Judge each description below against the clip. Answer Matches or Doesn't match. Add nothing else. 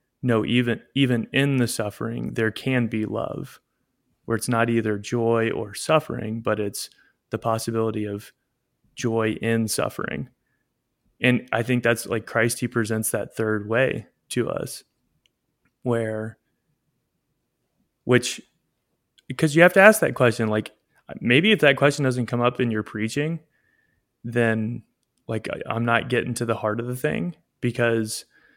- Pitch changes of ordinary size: Doesn't match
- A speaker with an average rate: Matches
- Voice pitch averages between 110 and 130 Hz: Matches